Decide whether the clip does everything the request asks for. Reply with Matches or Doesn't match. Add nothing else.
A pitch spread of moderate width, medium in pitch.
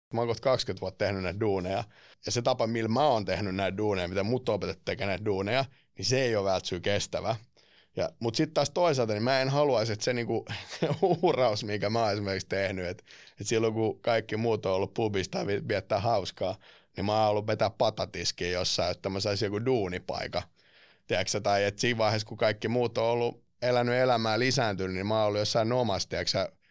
Doesn't match